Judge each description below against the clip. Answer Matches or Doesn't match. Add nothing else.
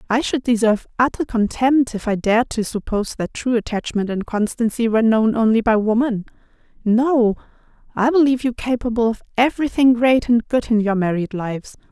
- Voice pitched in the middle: Doesn't match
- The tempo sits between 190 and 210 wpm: Doesn't match